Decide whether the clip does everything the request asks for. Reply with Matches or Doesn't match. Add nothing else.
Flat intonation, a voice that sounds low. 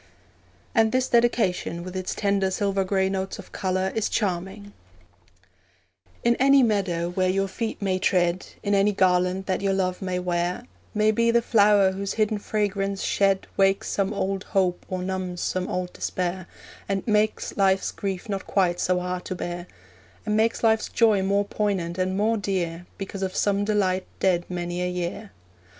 Doesn't match